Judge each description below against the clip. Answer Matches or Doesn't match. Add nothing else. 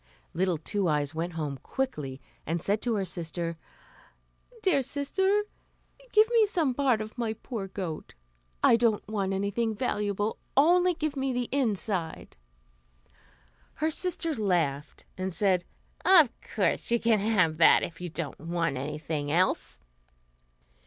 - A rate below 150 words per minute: Matches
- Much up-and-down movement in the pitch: Matches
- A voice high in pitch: Matches